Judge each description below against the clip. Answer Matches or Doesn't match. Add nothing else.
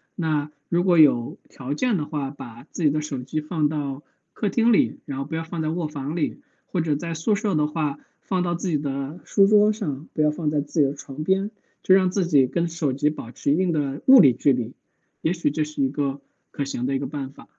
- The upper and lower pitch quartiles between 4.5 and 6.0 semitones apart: Doesn't match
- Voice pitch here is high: Doesn't match